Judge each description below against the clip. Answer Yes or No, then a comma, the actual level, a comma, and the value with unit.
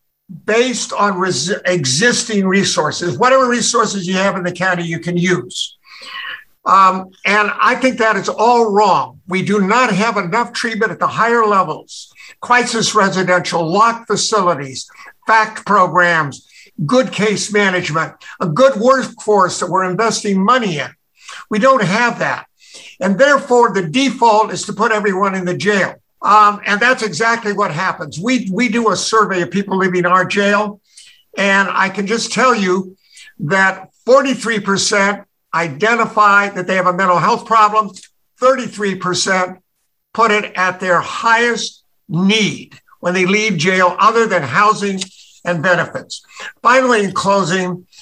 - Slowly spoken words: No, average, 150 wpm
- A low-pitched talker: No, high, 205 Hz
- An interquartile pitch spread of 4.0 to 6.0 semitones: No, average, 3.5 semitones